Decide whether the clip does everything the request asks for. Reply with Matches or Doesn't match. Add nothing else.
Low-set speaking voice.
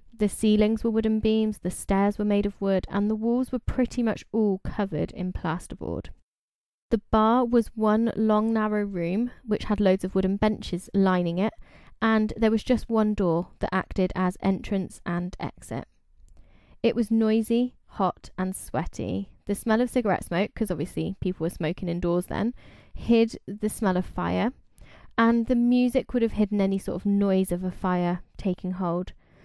Doesn't match